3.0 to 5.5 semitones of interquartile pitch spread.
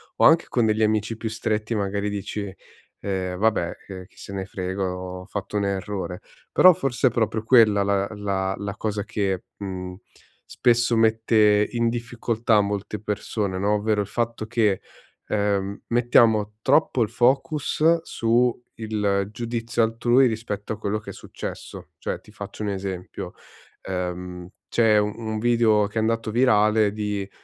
No: narrow, 2.4 semitones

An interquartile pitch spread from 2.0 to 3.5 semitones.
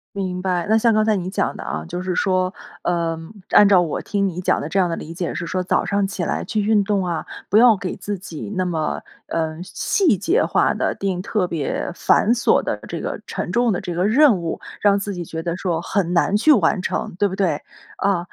Yes: average, 2.9 semitones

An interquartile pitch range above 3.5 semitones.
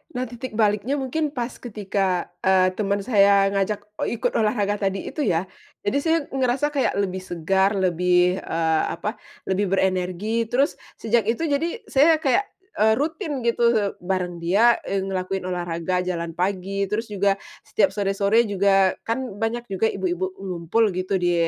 Yes: average, 4.1 semitones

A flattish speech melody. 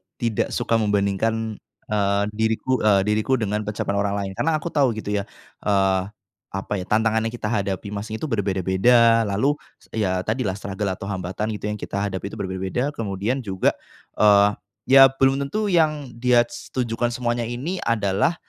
No: average, 3.3 semitones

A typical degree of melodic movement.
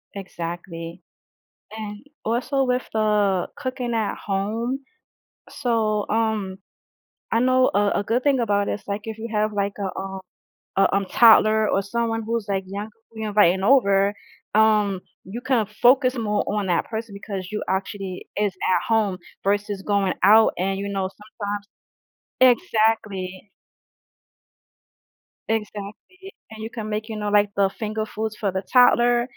No: narrow, 2.3 semitones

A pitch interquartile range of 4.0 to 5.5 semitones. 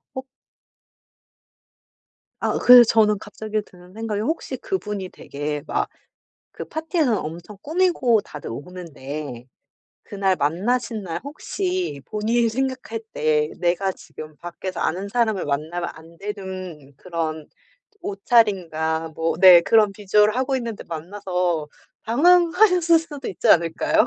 No: wide, 6.2 semitones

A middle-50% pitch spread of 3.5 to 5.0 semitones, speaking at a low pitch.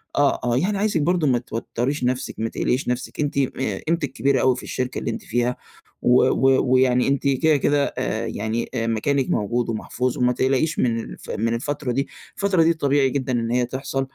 No: average, 2.7 semitones; low, 130 Hz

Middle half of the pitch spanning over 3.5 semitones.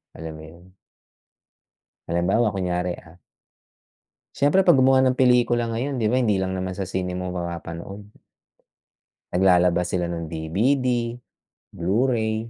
Yes: wide, 5.5 semitones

